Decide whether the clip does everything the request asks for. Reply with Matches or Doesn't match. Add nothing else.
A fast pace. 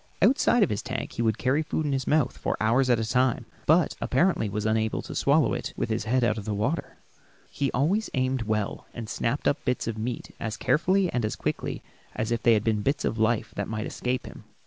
Matches